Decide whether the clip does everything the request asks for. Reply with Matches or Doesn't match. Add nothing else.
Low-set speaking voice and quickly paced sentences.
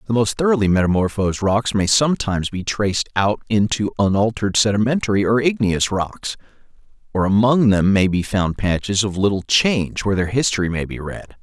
Doesn't match